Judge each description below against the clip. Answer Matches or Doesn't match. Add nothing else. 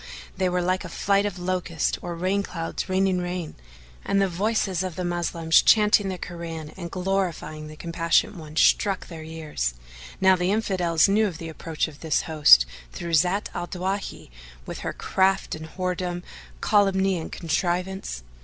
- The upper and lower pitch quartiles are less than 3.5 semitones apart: Matches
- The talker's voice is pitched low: Doesn't match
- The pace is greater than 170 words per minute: Doesn't match